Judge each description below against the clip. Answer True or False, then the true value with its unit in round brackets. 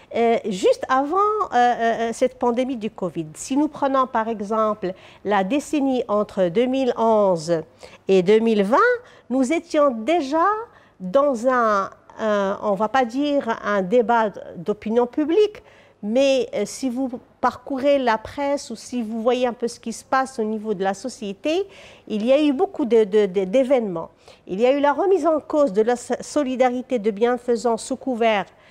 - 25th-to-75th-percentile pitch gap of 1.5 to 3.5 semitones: False (4.3 semitones)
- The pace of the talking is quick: False (165 wpm)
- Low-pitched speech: False (245 Hz)